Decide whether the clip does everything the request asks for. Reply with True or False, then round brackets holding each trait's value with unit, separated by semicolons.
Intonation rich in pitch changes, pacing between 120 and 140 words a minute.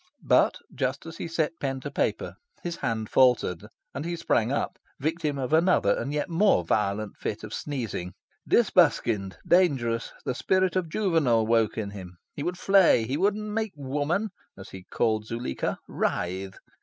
False (7.3 semitones; 165 wpm)